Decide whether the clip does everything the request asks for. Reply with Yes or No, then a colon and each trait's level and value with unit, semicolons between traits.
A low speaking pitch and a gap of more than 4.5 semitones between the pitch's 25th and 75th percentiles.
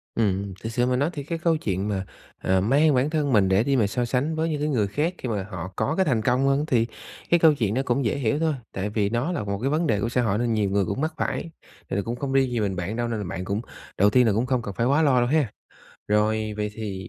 Yes: low, 120 Hz; average, 5.3 semitones